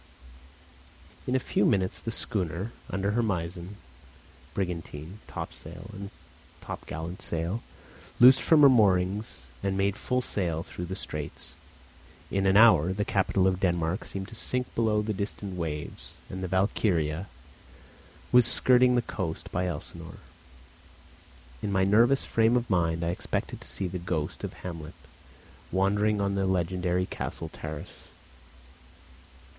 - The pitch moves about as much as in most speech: Yes, average, 3.4 semitones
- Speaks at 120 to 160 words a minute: Yes, average, 140 wpm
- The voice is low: Yes, very low, 95 Hz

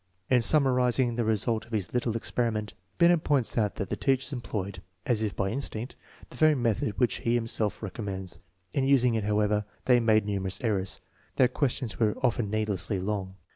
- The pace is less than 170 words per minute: No, average, 175 wpm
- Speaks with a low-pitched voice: Yes, low, 115 Hz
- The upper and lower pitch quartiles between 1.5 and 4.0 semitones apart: Yes, average, 3.1 semitones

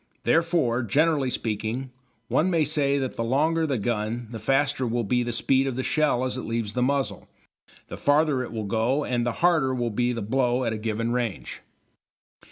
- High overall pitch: No, low, 125 Hz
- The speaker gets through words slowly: No, average, 195 wpm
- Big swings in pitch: No, average, 3.4 semitones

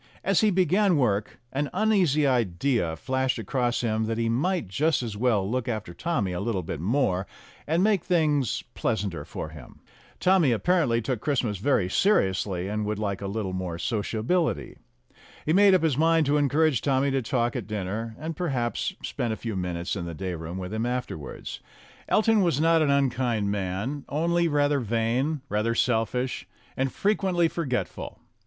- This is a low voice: Yes, low, 125 Hz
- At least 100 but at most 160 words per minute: No, average, 170 wpm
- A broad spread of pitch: Yes, wide, 6.9 semitones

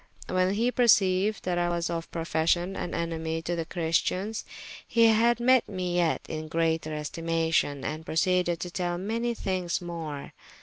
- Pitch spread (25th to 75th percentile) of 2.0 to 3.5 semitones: Yes, average, 2.9 semitones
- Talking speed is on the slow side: No, average, 160 wpm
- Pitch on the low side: No, medium, 175 Hz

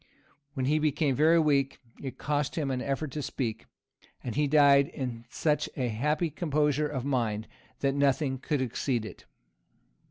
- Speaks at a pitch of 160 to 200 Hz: No, medium, 140 Hz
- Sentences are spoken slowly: No, average, 160 wpm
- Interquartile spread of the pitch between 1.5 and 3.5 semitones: Yes, narrow, 2.6 semitones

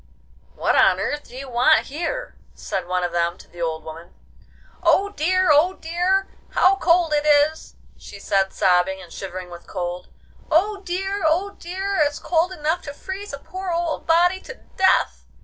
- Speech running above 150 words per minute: Yes, average, 175 wpm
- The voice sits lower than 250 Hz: No, very high, 315 Hz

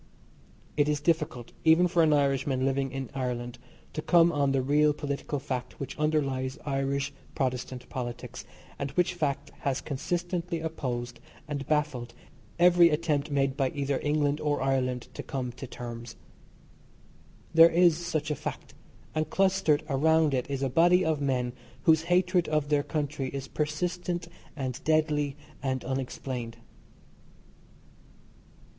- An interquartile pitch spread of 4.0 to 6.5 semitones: No, average, 3.2 semitones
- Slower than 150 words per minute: Yes, average, 140 wpm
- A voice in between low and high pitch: Yes, medium, 145 Hz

